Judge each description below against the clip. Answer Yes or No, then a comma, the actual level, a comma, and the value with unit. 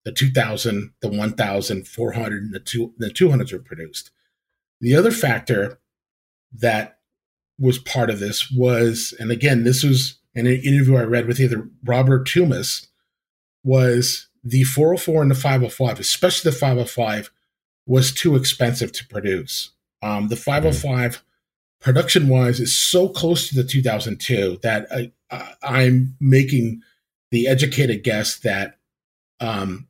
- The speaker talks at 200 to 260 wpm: No, slow, 135 wpm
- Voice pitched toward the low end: Yes, low, 125 Hz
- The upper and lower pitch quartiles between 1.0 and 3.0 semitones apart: Yes, narrow, 2.6 semitones